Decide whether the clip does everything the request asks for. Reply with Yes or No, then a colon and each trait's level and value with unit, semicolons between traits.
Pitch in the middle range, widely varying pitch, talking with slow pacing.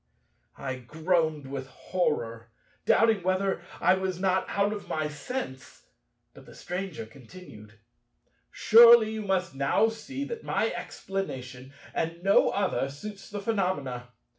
Yes: medium, 180 Hz; wide, 6.8 semitones; slow, 130 wpm